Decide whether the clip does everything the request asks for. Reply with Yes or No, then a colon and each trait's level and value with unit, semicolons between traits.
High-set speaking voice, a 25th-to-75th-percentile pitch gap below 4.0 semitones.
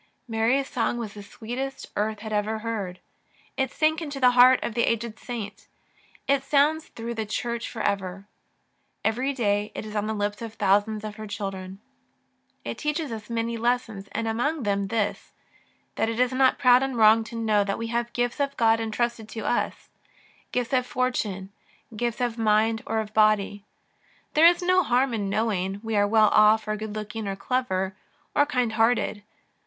Yes: high, 225 Hz; average, 2.8 semitones